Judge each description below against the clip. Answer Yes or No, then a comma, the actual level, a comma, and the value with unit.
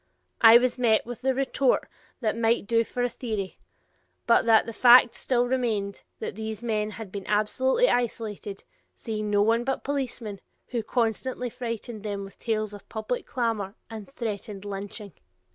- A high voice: Yes, high, 225 Hz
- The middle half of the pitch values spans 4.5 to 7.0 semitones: No, average, 2.7 semitones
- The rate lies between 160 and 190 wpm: Yes, average, 165 wpm